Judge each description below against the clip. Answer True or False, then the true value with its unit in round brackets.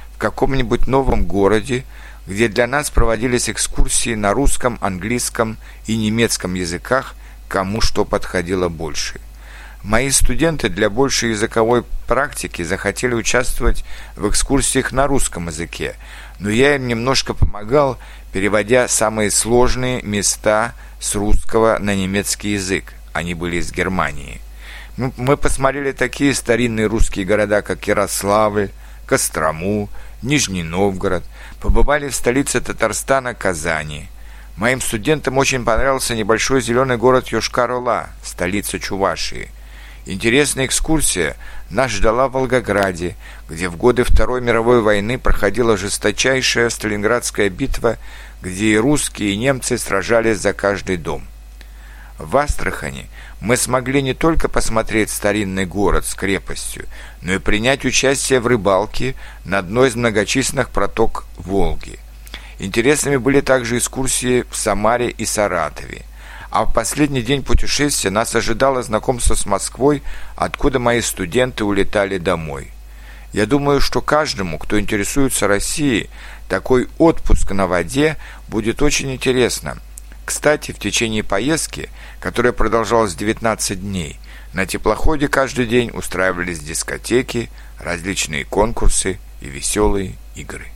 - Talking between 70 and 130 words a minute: True (120 wpm)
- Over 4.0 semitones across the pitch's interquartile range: True (4.8 semitones)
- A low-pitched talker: True (110 Hz)